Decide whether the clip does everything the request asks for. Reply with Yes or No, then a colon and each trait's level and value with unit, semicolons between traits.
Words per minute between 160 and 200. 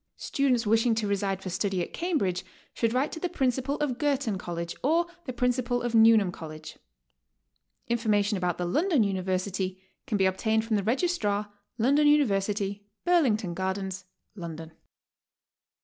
No: average, 150 wpm